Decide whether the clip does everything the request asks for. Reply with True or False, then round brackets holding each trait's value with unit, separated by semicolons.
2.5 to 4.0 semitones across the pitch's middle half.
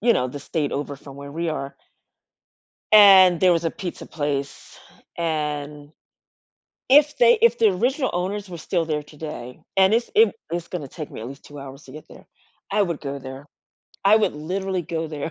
False (4.9 semitones)